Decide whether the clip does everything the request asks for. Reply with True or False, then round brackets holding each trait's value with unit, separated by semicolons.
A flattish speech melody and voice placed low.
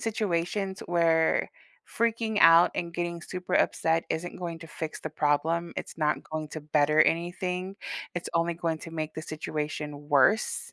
False (2.2 semitones; 165 Hz)